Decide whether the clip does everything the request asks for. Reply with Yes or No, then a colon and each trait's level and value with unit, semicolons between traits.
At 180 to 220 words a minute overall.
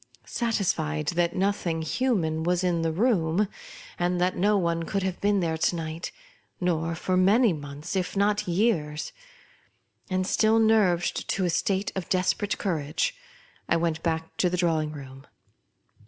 No: average, 155 wpm